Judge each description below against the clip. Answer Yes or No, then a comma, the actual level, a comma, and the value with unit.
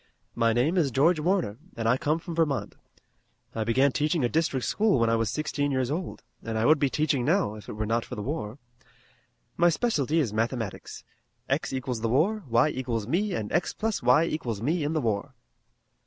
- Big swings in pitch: Yes, wide, 5.8 semitones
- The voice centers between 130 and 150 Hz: Yes, low, 135 Hz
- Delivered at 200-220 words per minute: Yes, fast, 205 wpm